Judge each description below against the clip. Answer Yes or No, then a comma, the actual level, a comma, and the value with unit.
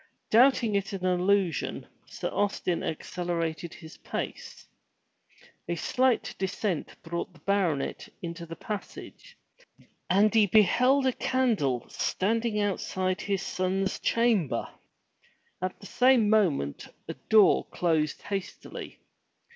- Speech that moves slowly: Yes, slow, 110 wpm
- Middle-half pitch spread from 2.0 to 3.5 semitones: No, average, 4.1 semitones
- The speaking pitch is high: Yes, high, 195 Hz